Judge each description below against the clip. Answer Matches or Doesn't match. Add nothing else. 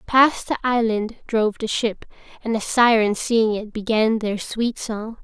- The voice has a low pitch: Doesn't match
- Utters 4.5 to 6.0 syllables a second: Doesn't match